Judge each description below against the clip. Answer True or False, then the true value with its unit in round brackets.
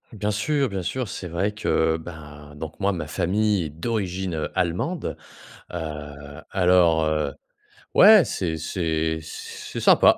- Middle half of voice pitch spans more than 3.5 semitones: True (4.1 semitones)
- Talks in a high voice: False (85 Hz)